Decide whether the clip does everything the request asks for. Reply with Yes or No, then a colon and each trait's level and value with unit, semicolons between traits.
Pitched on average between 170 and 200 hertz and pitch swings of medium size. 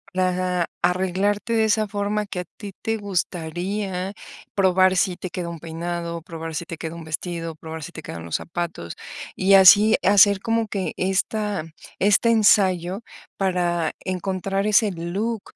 Yes: medium, 185 Hz; average, 3.0 semitones